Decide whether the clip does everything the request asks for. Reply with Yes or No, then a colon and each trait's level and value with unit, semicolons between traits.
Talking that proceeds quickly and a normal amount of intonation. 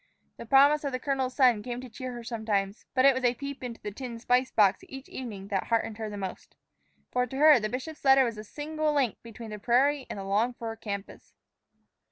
Yes: fast, 225 wpm; average, 3.6 semitones